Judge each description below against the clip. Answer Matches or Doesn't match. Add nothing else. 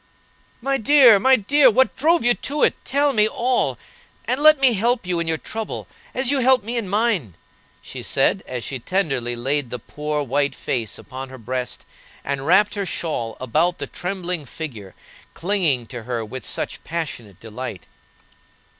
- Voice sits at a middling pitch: Matches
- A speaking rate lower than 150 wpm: Doesn't match